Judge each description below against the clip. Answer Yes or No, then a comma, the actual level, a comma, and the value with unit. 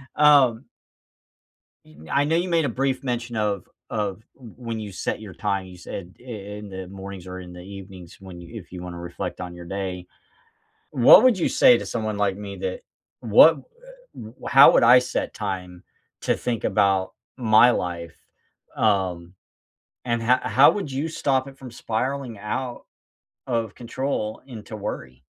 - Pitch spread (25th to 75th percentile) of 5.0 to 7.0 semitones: Yes, wide, 5.4 semitones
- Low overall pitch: Yes, low, 110 Hz